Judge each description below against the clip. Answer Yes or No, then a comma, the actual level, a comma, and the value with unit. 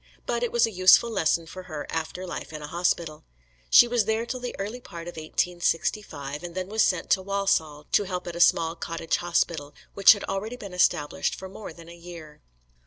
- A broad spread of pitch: No, average, 3.5 semitones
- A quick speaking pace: Yes, fast, 210 wpm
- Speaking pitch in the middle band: Yes, medium, 175 Hz